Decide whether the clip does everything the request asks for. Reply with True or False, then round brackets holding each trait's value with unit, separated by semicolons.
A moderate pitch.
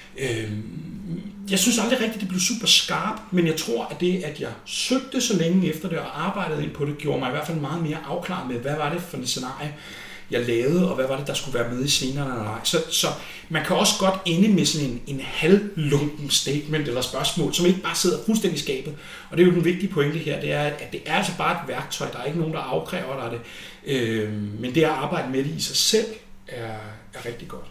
True (155 Hz)